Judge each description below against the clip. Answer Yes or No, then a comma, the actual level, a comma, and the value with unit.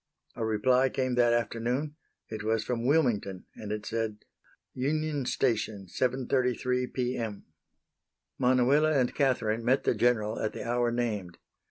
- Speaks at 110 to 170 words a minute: Yes, average, 140 wpm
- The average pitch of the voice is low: Yes, low, 120 Hz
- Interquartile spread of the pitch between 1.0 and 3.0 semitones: Yes, average, 2.7 semitones